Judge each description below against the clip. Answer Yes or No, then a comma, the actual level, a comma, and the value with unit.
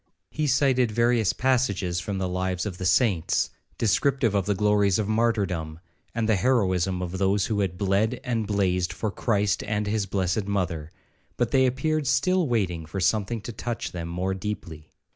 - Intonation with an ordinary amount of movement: Yes, average, 4.1 semitones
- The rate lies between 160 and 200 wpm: Yes, average, 175 wpm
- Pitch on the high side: No, low, 100 Hz